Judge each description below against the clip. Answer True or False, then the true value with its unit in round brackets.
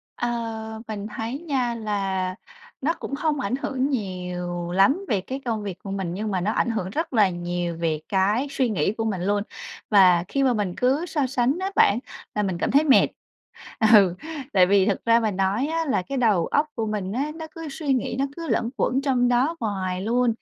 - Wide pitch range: True (5.8 semitones)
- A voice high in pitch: True (220 Hz)